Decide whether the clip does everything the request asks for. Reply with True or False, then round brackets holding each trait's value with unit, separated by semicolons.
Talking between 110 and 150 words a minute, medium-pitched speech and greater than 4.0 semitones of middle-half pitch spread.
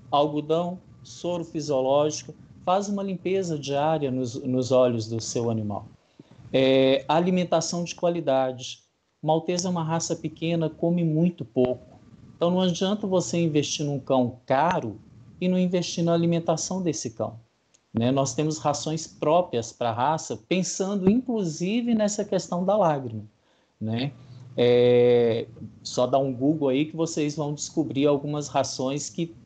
True (140 wpm; 150 Hz; 5.2 semitones)